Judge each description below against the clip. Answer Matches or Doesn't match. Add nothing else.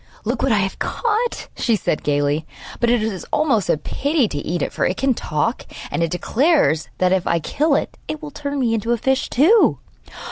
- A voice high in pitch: Matches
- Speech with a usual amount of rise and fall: Doesn't match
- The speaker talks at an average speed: Doesn't match